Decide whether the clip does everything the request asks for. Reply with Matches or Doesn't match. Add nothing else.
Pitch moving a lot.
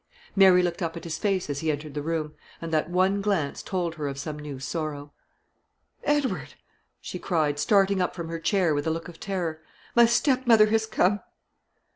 Doesn't match